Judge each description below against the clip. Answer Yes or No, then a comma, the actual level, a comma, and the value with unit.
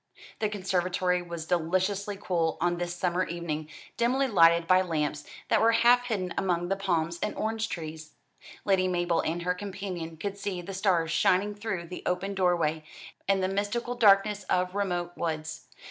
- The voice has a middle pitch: Yes, medium, 180 Hz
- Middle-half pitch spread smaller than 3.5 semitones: Yes, average, 2.8 semitones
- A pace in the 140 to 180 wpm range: Yes, average, 165 wpm